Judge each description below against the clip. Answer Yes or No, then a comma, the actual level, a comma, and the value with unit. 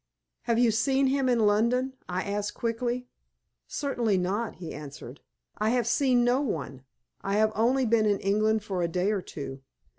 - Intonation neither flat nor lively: Yes, average, 3.8 semitones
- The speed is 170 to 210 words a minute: Yes, average, 175 wpm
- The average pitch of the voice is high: Yes, high, 220 Hz